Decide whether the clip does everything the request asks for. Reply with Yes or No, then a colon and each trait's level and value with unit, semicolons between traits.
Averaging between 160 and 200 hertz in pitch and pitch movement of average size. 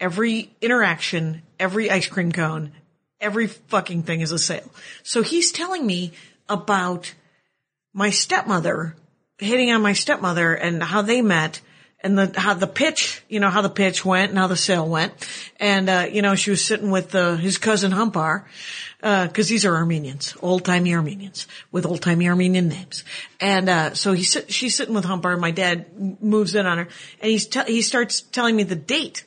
Yes: high, 190 Hz; average, 3.5 semitones